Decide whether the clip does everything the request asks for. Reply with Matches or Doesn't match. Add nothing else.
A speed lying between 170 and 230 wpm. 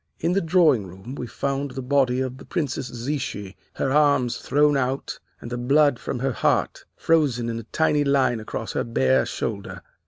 Matches